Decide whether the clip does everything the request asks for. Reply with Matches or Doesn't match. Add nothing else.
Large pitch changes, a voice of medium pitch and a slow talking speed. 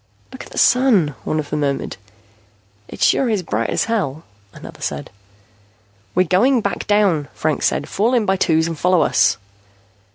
Doesn't match